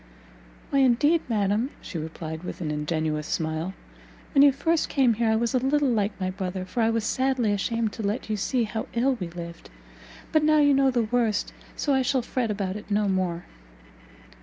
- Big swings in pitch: Yes, wide, 5.8 semitones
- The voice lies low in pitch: No, high, 220 Hz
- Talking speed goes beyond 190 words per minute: Yes, average, 200 wpm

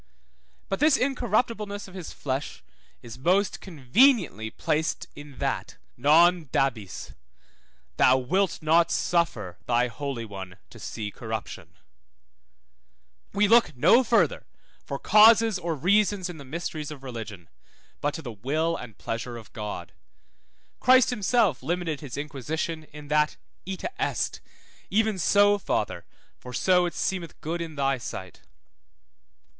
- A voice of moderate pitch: Yes, medium, 160 Hz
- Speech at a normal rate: No, slow, 130 wpm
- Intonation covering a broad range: Yes, wide, 7.3 semitones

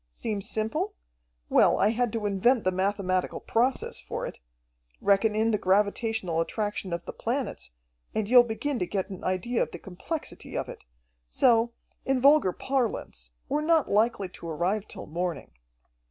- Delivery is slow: No, average, 160 wpm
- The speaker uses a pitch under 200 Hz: No, high, 210 Hz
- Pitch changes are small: No, average, 4.3 semitones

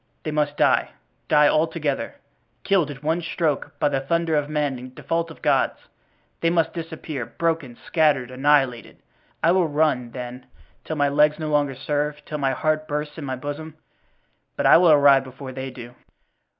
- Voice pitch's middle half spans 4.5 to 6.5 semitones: No, average, 2.9 semitones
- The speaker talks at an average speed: Yes, average, 170 wpm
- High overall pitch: No, medium, 150 Hz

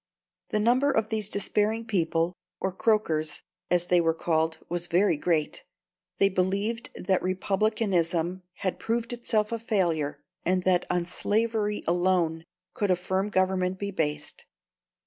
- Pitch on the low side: No, medium, 185 Hz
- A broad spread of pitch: No, average, 3.6 semitones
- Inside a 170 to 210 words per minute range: No, average, 140 wpm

